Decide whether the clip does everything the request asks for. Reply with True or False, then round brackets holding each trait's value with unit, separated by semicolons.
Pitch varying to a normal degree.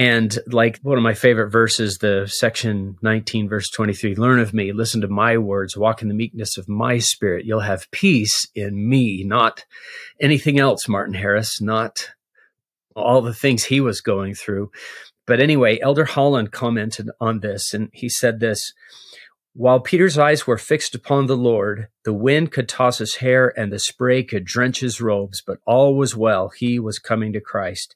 True (3.2 semitones)